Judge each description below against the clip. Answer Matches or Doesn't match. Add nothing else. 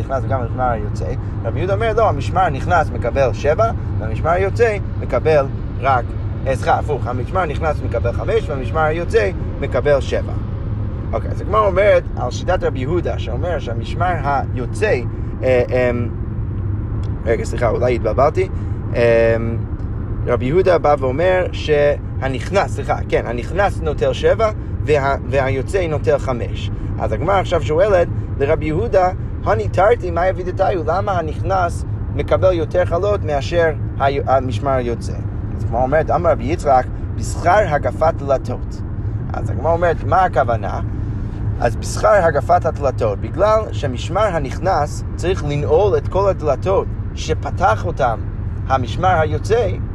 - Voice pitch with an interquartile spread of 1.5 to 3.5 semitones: Matches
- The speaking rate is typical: Matches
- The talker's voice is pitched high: Doesn't match